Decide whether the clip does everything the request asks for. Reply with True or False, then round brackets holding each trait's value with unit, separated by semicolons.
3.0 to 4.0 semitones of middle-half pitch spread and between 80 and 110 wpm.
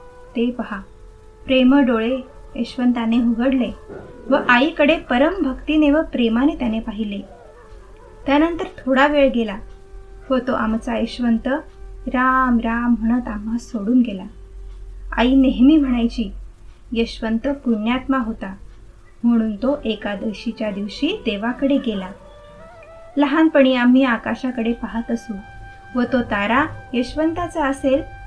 True (3.4 semitones; 100 wpm)